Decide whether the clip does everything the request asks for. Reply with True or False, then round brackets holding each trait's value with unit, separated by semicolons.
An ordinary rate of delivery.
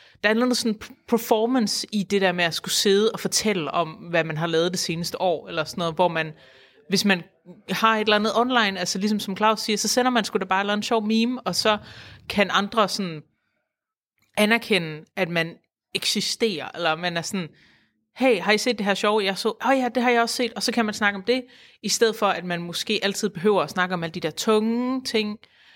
False (235 wpm)